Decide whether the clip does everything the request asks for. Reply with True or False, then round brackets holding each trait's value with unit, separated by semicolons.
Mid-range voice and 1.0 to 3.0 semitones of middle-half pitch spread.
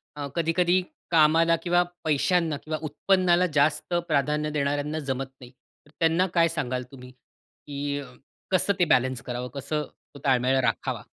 False (150 Hz; 3.6 semitones)